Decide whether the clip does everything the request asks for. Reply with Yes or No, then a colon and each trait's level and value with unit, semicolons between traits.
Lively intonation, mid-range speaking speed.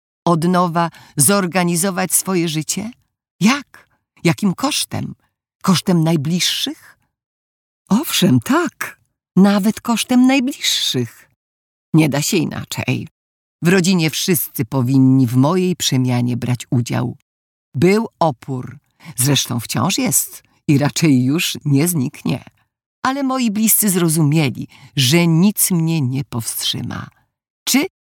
No: wide, 6.4 semitones; slow, 105 wpm